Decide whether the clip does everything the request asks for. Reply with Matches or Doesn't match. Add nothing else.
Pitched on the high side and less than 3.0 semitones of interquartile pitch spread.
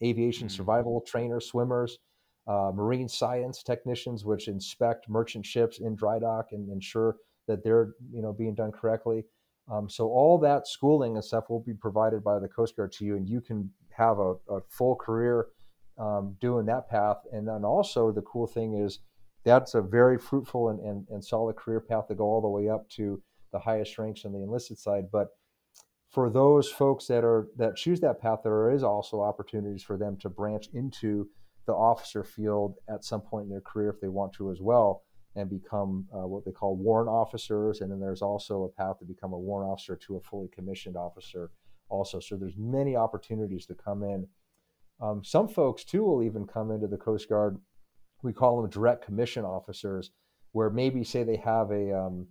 Doesn't match